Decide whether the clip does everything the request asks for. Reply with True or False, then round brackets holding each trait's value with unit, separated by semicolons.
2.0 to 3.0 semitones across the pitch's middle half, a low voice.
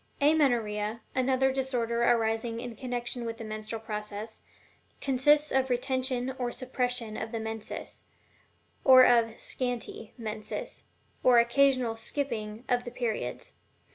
False (2.5 semitones; 240 Hz)